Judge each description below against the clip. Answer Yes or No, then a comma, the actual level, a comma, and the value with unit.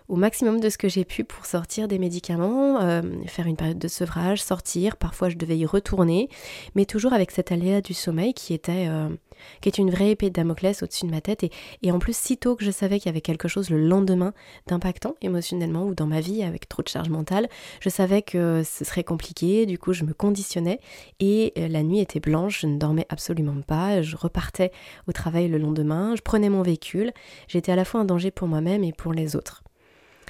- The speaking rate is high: Yes, fast, 225 wpm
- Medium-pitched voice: Yes, medium, 180 Hz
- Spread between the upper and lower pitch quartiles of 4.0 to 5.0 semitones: No, average, 3.0 semitones